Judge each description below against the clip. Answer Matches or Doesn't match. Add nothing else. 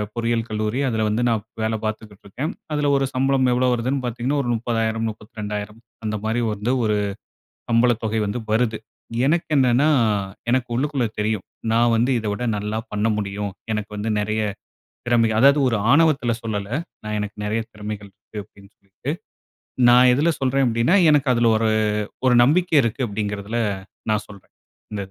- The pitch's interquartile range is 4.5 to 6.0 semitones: Doesn't match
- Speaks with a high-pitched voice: Doesn't match